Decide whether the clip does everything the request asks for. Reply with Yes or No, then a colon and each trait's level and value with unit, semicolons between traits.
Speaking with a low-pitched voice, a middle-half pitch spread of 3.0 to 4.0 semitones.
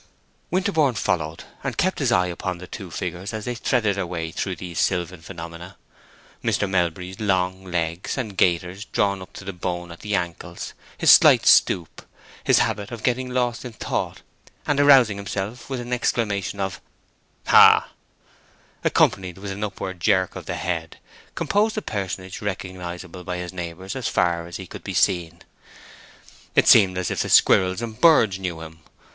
Yes: very low, 95 Hz; average, 3.3 semitones